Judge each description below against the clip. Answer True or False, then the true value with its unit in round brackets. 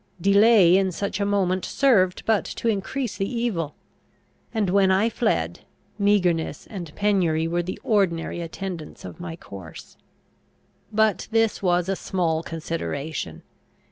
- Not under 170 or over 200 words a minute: False (135 wpm)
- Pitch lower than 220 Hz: True (190 Hz)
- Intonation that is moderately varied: True (3.7 semitones)